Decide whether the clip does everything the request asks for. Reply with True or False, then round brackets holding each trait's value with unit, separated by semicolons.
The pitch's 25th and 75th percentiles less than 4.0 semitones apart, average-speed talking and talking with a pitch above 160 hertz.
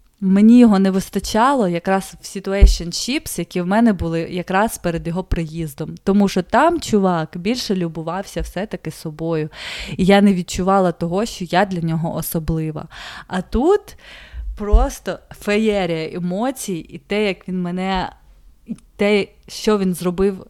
True (3.3 semitones; 145 wpm; 190 Hz)